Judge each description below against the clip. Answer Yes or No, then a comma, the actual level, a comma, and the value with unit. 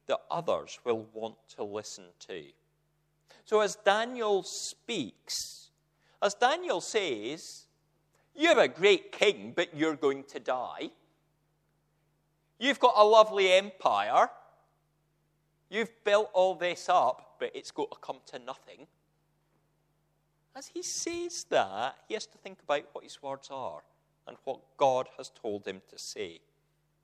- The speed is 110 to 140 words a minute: Yes, slow, 135 wpm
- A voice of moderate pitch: Yes, medium, 180 Hz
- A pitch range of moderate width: No, wide, 7.0 semitones